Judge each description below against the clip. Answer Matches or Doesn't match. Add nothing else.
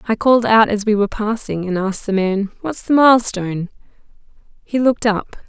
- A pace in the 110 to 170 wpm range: Doesn't match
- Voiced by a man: Doesn't match